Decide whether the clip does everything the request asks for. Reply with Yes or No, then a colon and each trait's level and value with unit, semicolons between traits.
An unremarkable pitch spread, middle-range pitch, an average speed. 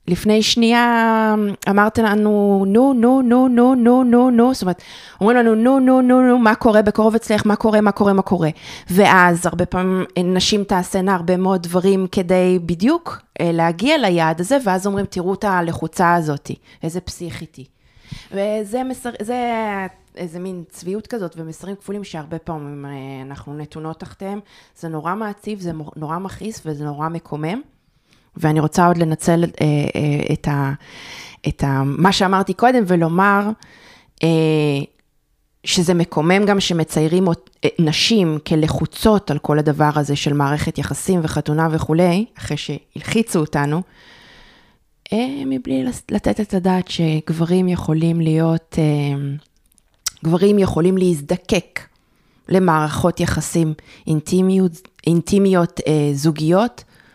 Yes: average, 4.7 semitones; medium, 180 Hz; average, 130 wpm